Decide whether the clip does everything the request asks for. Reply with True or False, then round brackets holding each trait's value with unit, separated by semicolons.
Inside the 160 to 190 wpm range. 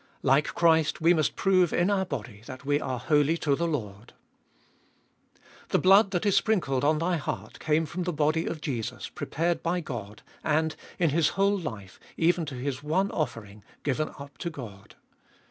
True (180 wpm)